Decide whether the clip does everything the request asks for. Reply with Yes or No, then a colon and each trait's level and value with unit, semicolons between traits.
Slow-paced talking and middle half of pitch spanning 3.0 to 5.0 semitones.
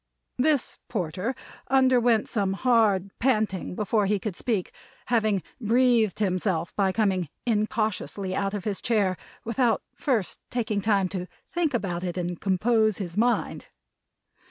Yes: slow, 130 wpm; average, 3.6 semitones